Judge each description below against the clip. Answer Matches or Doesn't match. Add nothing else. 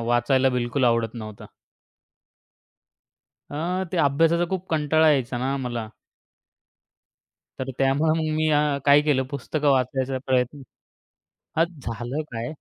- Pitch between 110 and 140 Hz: Matches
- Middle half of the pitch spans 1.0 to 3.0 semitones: Doesn't match